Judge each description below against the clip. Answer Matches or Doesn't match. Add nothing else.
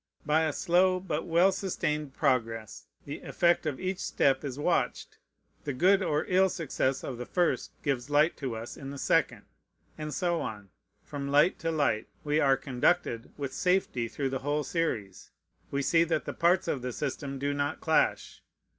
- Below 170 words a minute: Doesn't match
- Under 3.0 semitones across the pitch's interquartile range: Doesn't match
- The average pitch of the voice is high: Doesn't match